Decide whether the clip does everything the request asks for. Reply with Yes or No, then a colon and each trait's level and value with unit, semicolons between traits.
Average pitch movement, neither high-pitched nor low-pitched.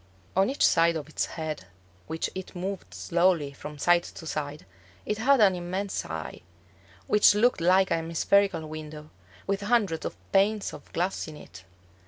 Yes: average, 4.0 semitones; medium, 175 Hz